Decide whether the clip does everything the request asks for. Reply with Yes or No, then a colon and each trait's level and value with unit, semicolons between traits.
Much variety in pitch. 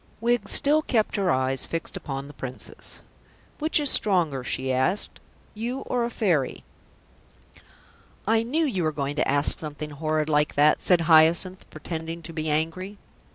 Yes: wide, 6.1 semitones